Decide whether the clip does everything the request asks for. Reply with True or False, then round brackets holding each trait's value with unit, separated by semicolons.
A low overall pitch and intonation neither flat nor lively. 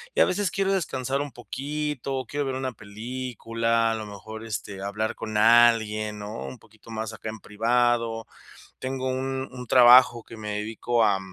True (115 Hz; 3.1 semitones)